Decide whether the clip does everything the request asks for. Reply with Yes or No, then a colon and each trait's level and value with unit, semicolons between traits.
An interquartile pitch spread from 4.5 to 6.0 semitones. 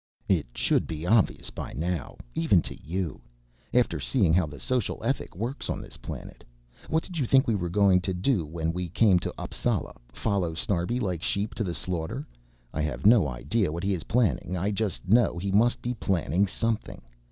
Yes: average, 5.1 semitones